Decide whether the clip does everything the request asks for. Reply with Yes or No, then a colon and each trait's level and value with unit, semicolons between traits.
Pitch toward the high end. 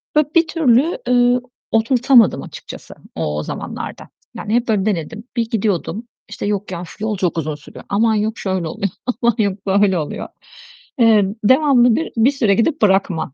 Yes: high, 215 Hz